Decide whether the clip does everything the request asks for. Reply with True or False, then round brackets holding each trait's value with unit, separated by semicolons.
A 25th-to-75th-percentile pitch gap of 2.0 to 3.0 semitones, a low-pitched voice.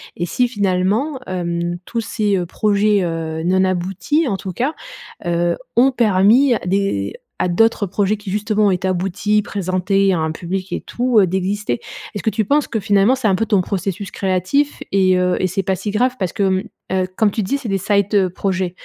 False (2.7 semitones; 195 Hz)